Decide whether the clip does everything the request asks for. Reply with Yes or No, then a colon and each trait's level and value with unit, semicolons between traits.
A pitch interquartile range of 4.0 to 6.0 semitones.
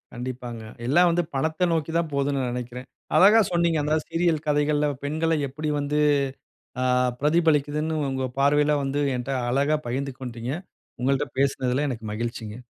No: average, 3.5 semitones